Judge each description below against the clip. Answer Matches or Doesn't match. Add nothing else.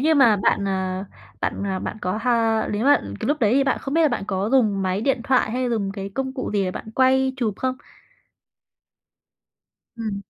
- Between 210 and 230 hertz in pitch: Matches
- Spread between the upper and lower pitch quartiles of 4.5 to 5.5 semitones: Matches